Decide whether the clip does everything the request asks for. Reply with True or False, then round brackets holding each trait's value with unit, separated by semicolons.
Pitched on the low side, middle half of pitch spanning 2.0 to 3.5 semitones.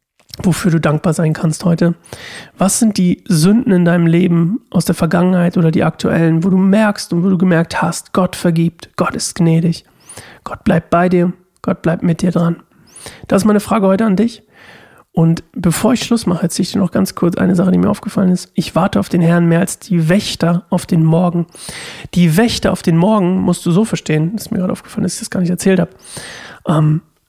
False (180 Hz; 2.4 semitones)